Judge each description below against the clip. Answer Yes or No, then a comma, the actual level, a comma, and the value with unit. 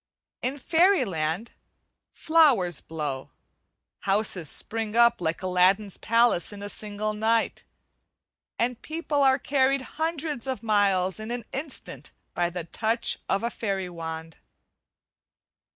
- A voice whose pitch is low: No, high, 215 Hz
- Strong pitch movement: Yes, wide, 6.2 semitones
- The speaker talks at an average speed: No, slow, 120 wpm